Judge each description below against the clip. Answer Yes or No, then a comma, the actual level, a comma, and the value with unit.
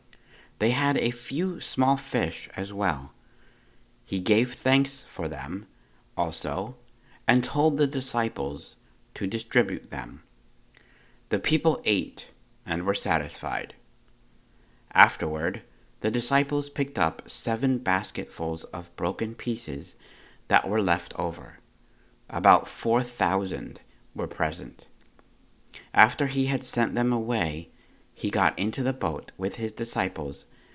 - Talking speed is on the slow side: Yes, slow, 115 wpm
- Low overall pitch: Yes, low, 115 Hz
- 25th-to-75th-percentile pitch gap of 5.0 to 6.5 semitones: Yes, wide, 5.5 semitones